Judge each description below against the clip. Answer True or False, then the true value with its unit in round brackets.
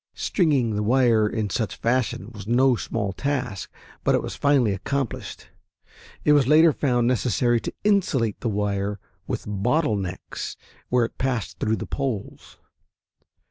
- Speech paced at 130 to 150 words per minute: True (145 wpm)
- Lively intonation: False (4.3 semitones)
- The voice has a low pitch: True (120 Hz)